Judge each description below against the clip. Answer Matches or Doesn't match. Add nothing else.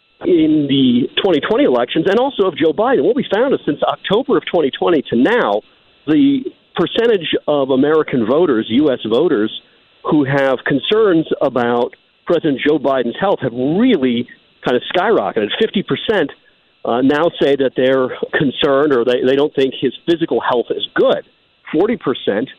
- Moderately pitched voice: Matches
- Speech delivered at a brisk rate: Doesn't match